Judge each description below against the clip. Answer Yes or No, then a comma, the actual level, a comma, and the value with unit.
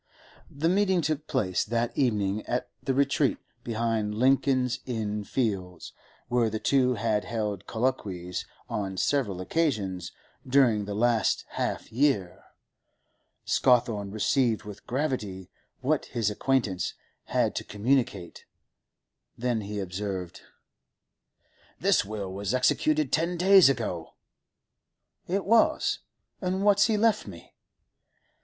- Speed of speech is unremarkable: No, slow, 115 wpm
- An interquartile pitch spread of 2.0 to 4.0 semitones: No, average, 5.2 semitones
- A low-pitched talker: Yes, low, 115 Hz